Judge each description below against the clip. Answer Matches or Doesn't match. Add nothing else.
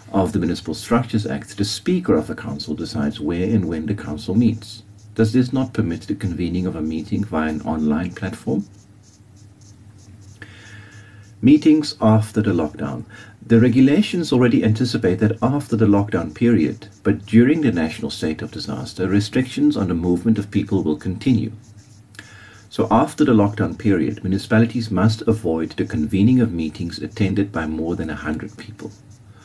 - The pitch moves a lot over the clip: Doesn't match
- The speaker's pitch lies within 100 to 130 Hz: Matches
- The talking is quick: Doesn't match